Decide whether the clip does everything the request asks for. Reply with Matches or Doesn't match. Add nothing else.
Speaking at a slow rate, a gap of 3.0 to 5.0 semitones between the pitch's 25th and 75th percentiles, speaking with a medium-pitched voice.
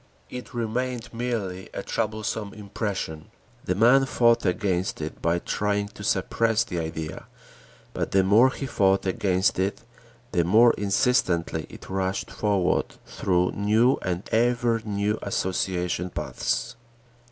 Doesn't match